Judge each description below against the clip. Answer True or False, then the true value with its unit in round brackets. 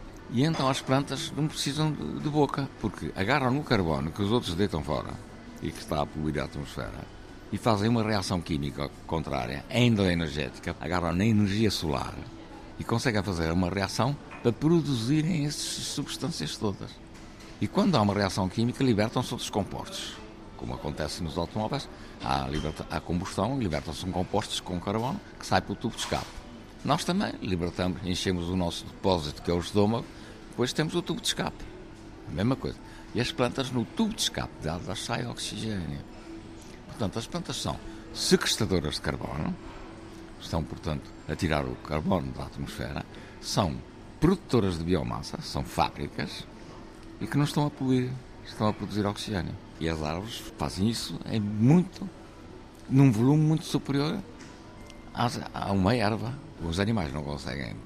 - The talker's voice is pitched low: True (105 Hz)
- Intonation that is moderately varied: False (6.7 semitones)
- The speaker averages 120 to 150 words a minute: False (160 wpm)